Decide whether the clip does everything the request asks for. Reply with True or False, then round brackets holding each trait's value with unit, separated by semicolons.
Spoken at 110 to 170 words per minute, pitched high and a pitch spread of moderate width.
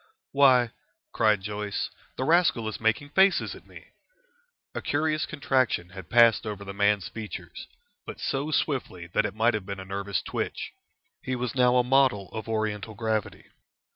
False (165 wpm; 110 Hz; 4.2 semitones)